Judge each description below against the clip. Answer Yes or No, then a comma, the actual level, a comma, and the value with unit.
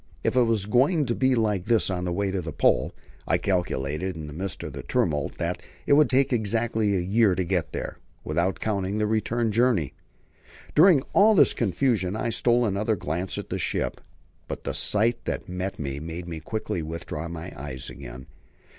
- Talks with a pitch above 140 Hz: No, low, 100 Hz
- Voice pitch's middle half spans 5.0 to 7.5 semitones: Yes, wide, 5.4 semitones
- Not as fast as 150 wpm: No, average, 195 wpm